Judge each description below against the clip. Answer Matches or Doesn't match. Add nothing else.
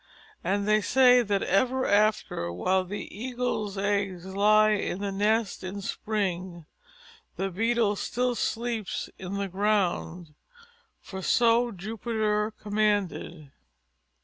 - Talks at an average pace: Doesn't match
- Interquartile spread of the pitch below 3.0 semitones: Matches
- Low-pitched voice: Doesn't match